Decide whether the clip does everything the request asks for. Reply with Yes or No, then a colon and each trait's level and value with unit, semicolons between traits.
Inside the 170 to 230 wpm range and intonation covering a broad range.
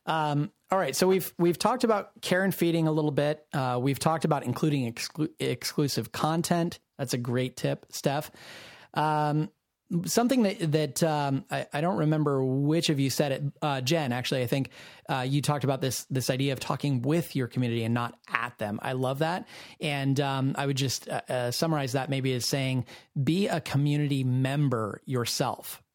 No: average, 190 wpm; average, 3.6 semitones